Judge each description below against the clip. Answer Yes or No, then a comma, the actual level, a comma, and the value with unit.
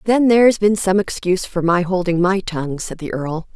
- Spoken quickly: Yes, fast, 220 wpm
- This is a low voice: No, medium, 185 Hz